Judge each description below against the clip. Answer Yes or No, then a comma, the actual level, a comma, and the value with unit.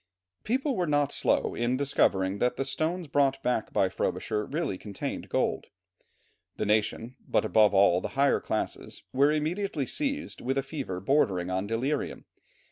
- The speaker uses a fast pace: No, average, 155 wpm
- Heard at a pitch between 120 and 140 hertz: Yes, low, 135 Hz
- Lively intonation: Yes, wide, 6.2 semitones